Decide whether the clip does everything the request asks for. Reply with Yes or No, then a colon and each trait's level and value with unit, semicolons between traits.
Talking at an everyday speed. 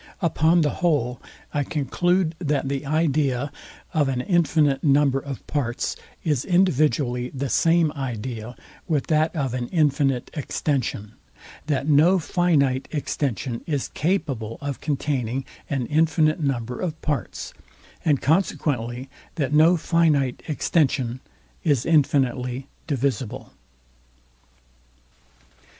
No: slow, 110 wpm